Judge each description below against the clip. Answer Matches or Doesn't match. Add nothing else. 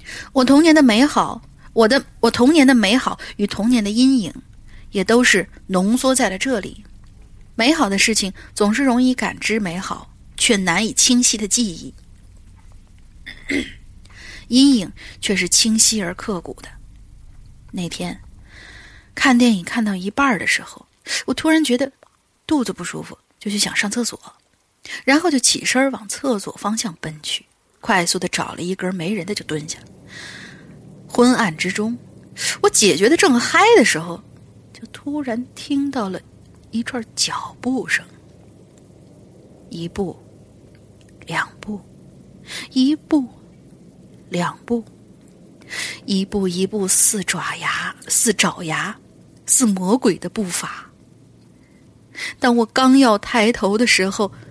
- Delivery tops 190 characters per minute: Doesn't match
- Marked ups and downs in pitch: Matches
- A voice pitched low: Doesn't match